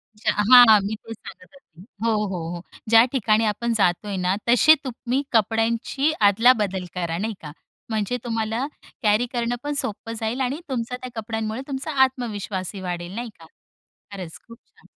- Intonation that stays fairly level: No, average, 3.4 semitones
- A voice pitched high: Yes, high, 225 Hz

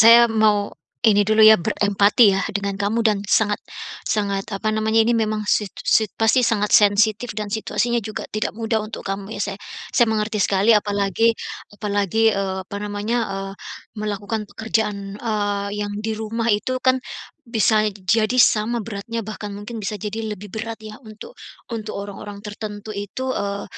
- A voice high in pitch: Yes, high, 210 Hz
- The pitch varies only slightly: Yes, narrow, 1.6 semitones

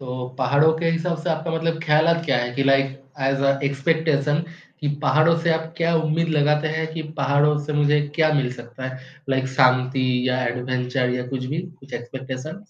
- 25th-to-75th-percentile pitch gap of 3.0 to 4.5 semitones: Yes, average, 3.7 semitones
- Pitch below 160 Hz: Yes, medium, 140 Hz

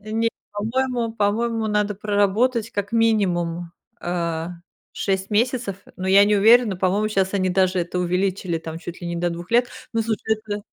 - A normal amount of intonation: Yes, average, 3.6 semitones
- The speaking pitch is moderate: No, high, 205 Hz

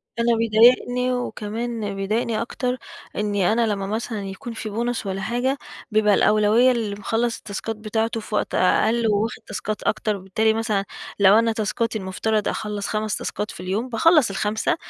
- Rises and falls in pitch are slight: Yes, narrow, 2.1 semitones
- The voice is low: No, high, 220 Hz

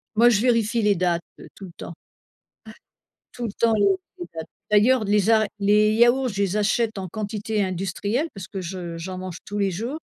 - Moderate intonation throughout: Yes, average, 3.2 semitones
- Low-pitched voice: No, high, 205 Hz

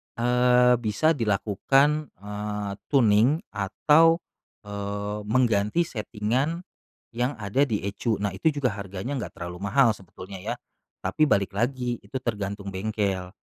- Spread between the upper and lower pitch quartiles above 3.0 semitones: Yes, average, 4.1 semitones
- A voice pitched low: Yes, low, 110 Hz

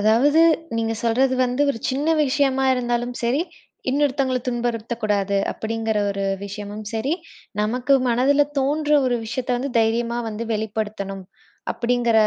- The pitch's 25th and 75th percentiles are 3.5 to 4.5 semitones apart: No, average, 3.0 semitones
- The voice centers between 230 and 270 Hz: Yes, high, 240 Hz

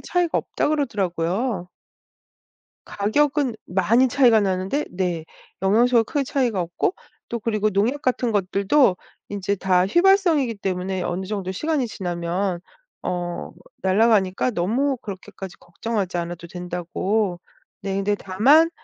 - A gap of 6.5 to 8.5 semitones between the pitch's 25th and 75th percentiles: No, average, 5.2 semitones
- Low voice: No, high, 200 Hz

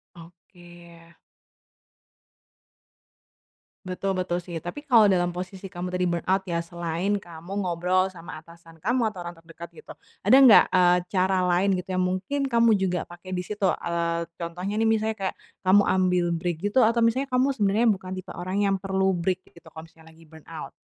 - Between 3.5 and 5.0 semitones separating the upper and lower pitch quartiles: No, narrow, 2.5 semitones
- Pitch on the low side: No, medium, 185 Hz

